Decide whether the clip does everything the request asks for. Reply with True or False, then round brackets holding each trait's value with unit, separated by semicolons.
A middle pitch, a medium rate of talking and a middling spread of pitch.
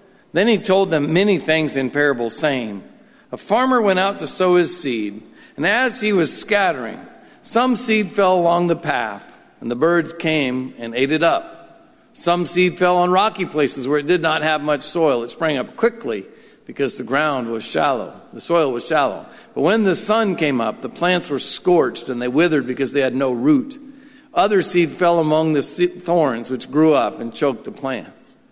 False (165 Hz; 195 wpm; 6.3 semitones)